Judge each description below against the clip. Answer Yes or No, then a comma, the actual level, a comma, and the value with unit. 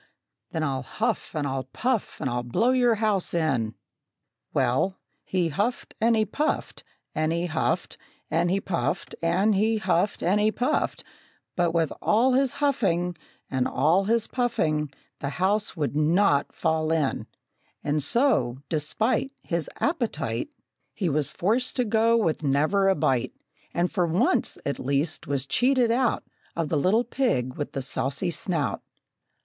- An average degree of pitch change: No, wide, 7.1 semitones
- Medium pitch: Yes, medium, 175 Hz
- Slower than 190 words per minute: Yes, average, 155 wpm